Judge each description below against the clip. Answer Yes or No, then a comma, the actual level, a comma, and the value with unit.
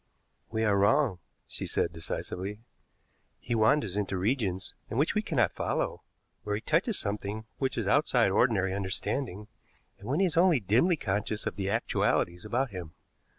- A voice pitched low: Yes, low, 110 Hz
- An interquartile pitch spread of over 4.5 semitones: Yes, average, 5.3 semitones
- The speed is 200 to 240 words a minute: No, average, 160 wpm